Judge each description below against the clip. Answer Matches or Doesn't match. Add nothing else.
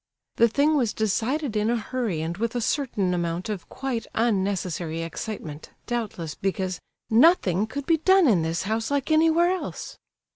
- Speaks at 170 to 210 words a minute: Doesn't match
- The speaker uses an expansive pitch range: Matches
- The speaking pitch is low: Doesn't match